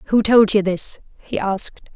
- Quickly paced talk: No, average, 185 wpm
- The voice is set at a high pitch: Yes, high, 205 Hz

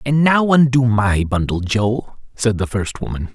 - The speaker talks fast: No, average, 180 wpm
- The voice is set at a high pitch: No, low, 120 Hz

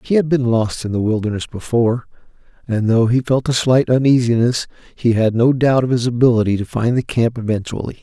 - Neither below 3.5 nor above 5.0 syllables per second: No, 5.6 syllables/s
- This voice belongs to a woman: No, male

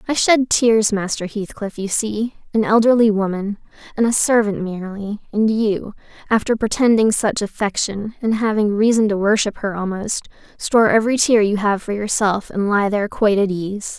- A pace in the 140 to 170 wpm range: Yes, average, 165 wpm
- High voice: Yes, high, 210 Hz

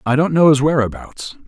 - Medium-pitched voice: Yes, medium, 145 Hz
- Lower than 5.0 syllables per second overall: No, 5.4 syllables/s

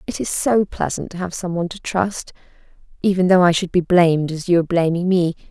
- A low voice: No, medium, 175 Hz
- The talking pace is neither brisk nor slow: No, fast, 230 wpm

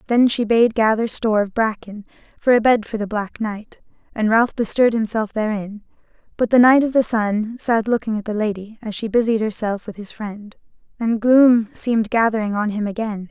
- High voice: Yes, high, 220 Hz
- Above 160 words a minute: Yes, average, 200 wpm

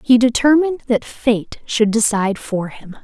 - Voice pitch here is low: No, high, 235 Hz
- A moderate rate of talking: Yes, average, 160 wpm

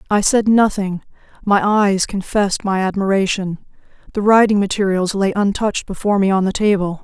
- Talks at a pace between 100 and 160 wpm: Yes, average, 155 wpm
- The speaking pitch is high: Yes, high, 200 Hz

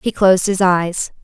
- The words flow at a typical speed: Yes, average, 195 wpm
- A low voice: No, medium, 185 Hz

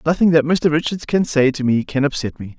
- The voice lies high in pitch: No, medium, 150 Hz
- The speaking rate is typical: No, fast, 255 wpm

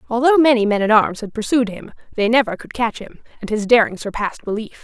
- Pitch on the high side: Yes, high, 225 Hz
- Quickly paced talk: Yes, fast, 225 wpm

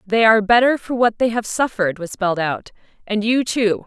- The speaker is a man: No, female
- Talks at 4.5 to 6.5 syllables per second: Yes, 5.6 syllables/s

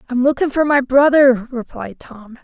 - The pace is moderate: Yes, average, 170 wpm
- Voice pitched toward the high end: Yes, very high, 260 Hz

